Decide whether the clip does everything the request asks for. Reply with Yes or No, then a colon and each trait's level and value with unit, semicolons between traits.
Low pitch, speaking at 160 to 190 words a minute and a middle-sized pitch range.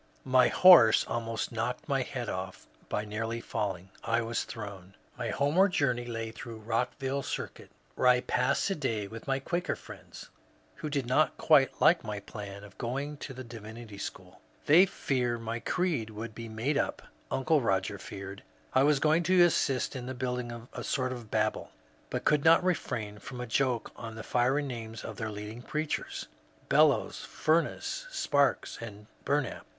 Yes: low, 120 Hz; average, 175 wpm; average, 4.2 semitones